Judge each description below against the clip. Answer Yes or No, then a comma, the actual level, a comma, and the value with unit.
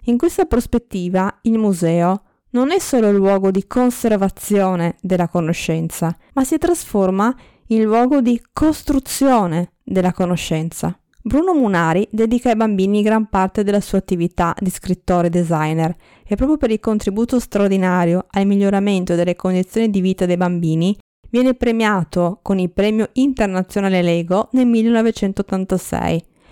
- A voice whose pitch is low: No, high, 200 Hz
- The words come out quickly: No, average, 135 wpm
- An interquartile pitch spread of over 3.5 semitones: Yes, average, 4.1 semitones